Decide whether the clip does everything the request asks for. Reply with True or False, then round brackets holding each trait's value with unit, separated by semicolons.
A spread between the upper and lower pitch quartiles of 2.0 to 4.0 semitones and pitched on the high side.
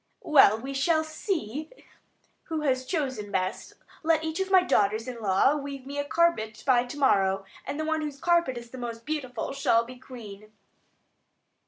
False (5.3 semitones; 265 Hz)